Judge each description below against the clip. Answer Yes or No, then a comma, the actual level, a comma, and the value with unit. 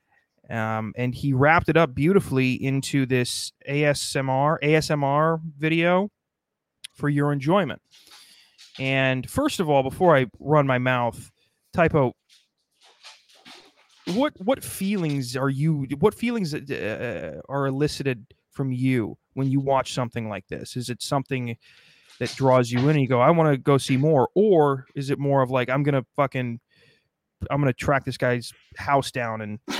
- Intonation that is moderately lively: Yes, average, 3.1 semitones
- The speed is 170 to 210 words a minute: No, average, 155 wpm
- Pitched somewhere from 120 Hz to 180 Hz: Yes, low, 135 Hz